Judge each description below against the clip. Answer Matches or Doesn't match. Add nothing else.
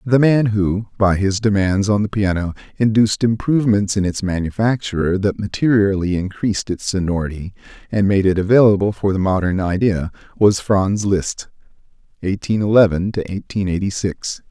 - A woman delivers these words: Doesn't match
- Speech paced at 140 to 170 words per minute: Matches